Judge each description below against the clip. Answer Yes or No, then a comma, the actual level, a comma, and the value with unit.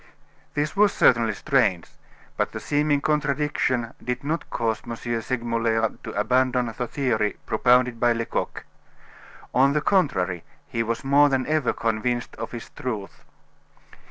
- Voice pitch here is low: Yes, low, 125 Hz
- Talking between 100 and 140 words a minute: Yes, slow, 135 wpm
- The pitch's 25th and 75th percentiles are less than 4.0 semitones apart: Yes, average, 3.6 semitones